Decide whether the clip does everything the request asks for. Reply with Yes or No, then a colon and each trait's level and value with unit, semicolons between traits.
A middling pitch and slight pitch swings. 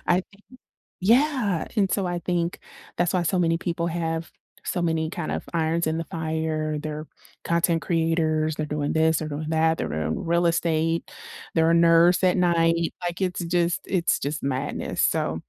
Yes: medium, 165 Hz; narrow, 1.6 semitones